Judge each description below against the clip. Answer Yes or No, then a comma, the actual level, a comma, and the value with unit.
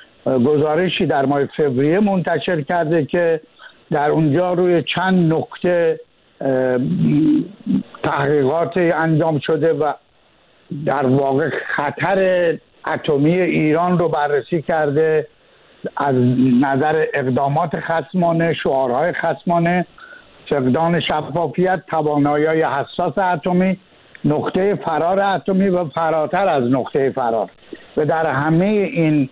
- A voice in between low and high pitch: Yes, medium, 160 Hz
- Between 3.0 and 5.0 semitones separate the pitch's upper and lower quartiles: Yes, average, 3.5 semitones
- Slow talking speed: Yes, slow, 100 wpm